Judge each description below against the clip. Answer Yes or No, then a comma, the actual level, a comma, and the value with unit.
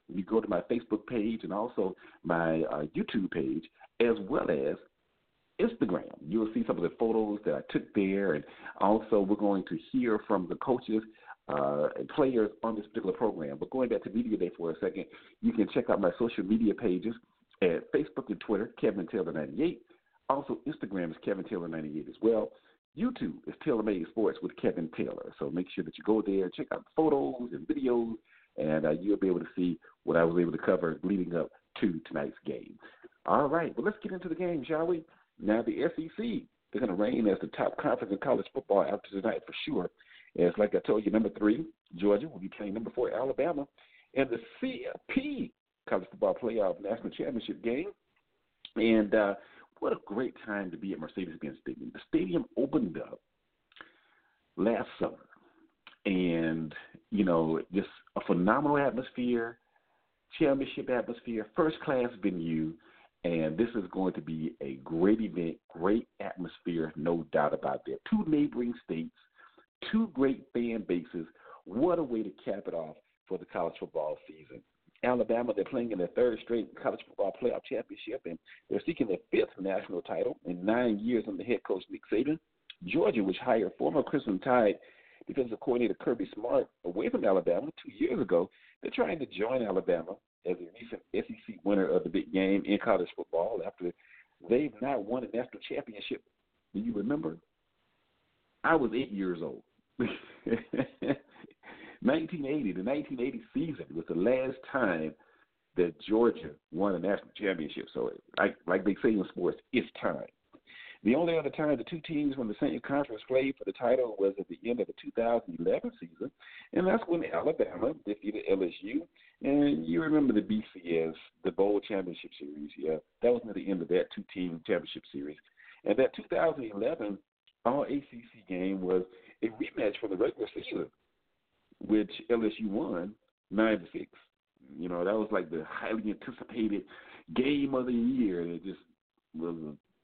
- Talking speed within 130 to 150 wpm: No, average, 175 wpm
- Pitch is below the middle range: Yes, low, 110 Hz